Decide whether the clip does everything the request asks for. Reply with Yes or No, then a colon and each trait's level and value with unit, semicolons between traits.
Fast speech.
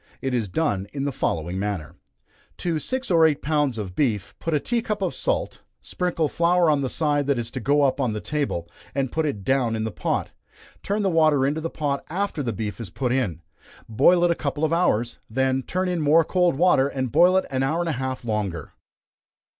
Yes: fast, 225 wpm